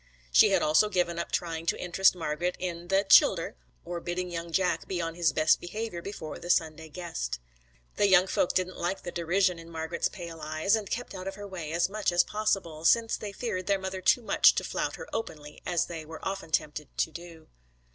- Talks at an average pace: No, fast, 215 wpm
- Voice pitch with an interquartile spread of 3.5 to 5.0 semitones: No, average, 2.9 semitones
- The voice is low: No, medium, 175 Hz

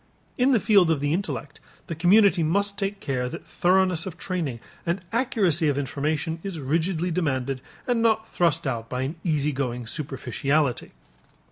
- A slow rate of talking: No, average, 160 wpm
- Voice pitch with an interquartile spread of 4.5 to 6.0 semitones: Yes, wide, 5.5 semitones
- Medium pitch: Yes, medium, 160 Hz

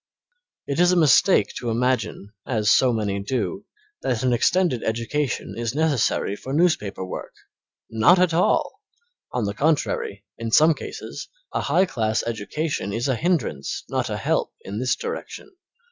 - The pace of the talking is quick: No, average, 155 wpm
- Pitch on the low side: Yes, low, 125 Hz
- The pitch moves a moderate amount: No, wide, 6.3 semitones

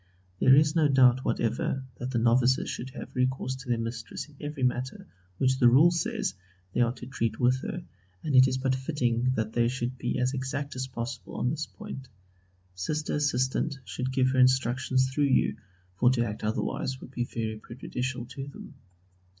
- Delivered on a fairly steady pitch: Yes, narrow, 1.8 semitones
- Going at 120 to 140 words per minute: No, average, 190 wpm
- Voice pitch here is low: Yes, low, 130 Hz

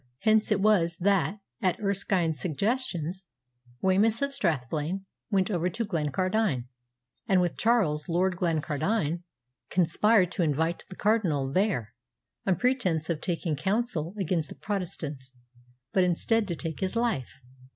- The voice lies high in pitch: No, medium, 180 Hz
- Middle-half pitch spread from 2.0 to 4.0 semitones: No, average, 4.6 semitones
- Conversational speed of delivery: No, slow, 130 wpm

